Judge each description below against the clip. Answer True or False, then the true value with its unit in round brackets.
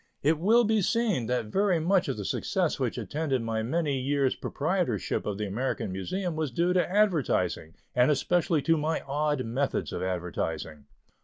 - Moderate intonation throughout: False (7.4 semitones)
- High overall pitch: False (145 Hz)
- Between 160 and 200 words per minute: True (170 wpm)